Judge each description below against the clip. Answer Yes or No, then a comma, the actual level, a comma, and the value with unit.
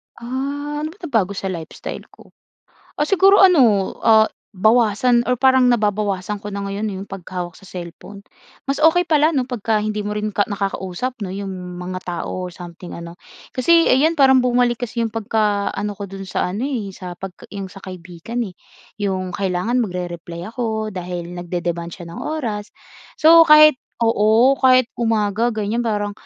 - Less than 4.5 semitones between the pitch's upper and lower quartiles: No, average, 5.0 semitones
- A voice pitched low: No, high, 210 Hz